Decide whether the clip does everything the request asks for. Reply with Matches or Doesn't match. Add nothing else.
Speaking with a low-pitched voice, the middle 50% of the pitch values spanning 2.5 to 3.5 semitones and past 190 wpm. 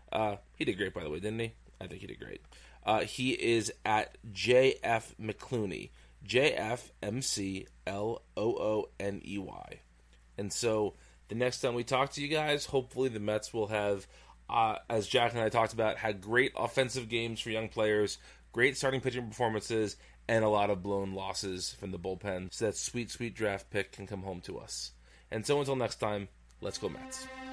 Doesn't match